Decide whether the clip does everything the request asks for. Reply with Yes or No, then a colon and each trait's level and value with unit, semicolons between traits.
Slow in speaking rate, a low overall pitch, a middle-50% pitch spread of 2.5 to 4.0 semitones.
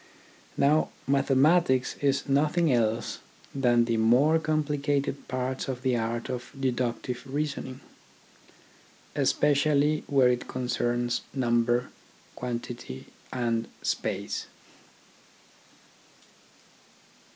Yes: slow, 85 wpm; low, 130 Hz; average, 2.8 semitones